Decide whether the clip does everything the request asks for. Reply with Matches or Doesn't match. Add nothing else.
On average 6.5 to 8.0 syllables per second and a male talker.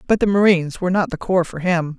Doesn't match